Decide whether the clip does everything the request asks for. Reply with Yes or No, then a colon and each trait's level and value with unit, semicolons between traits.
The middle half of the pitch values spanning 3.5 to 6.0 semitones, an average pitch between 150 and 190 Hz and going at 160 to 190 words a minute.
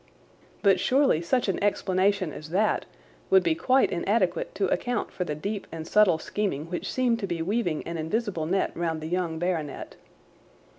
Yes: average, 4.5 semitones; medium, 185 Hz; average, 170 wpm